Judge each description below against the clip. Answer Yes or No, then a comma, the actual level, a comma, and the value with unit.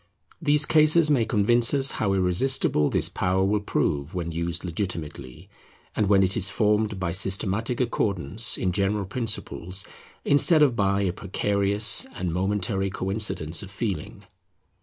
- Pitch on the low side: Yes, low, 100 Hz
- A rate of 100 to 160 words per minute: Yes, average, 140 wpm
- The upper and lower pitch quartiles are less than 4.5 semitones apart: Yes, average, 3.2 semitones